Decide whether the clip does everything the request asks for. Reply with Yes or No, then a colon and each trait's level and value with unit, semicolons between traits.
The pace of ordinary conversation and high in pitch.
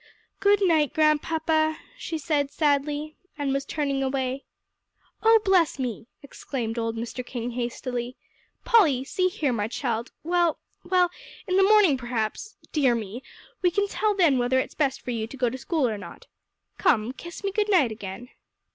Yes: average, 165 wpm; very high, 280 Hz